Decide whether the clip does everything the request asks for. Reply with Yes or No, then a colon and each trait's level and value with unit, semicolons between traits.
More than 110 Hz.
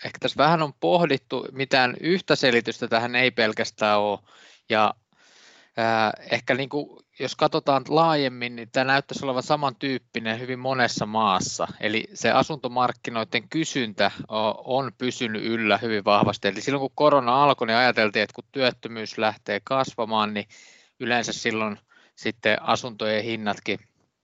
Yes: low, 120 Hz